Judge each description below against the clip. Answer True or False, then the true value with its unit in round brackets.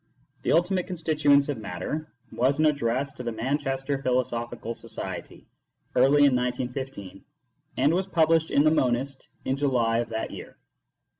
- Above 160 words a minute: False (155 wpm)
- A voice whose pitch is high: False (135 Hz)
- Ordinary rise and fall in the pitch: True (3.8 semitones)